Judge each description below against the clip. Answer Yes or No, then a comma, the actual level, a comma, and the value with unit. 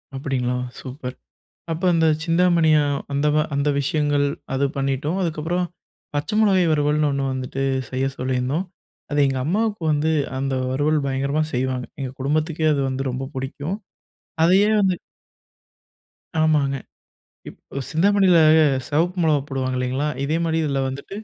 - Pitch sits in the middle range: Yes, medium, 145 Hz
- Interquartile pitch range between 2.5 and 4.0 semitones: Yes, average, 3.3 semitones